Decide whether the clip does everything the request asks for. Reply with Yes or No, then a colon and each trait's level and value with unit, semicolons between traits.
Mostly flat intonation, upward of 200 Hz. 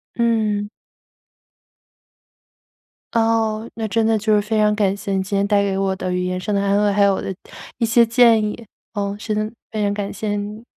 Yes: narrow, 1.8 semitones; high, 210 Hz